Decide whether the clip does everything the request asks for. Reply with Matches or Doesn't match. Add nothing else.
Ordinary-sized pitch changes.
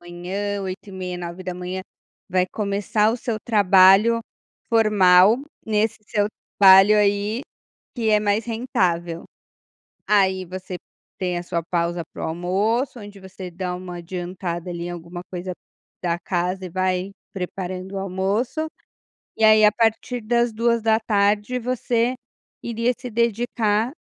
Matches